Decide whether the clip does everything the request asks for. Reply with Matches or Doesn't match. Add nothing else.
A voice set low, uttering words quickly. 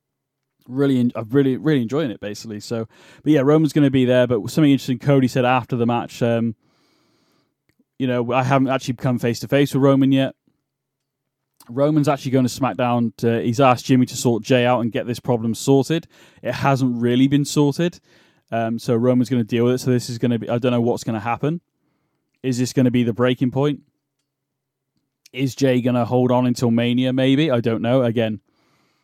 Matches